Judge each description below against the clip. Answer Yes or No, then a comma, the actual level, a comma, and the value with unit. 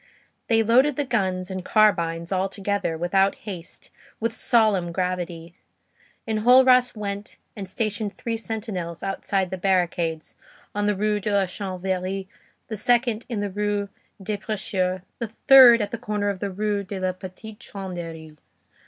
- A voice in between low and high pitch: No, high, 200 Hz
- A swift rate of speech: No, average, 155 wpm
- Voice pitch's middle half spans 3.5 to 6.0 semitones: No, average, 2.8 semitones